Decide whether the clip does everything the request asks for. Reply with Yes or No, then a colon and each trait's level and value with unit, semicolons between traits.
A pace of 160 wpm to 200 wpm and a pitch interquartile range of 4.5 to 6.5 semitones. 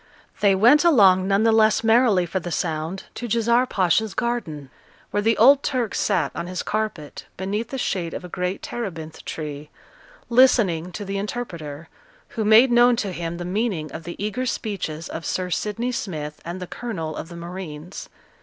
Yes: average, 180 wpm; average, 5.1 semitones